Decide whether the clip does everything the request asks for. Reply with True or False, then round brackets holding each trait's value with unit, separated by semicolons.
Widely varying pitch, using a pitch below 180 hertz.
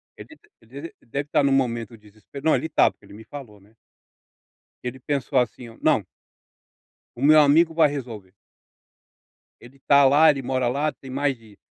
False (3.7 semitones; 135 Hz)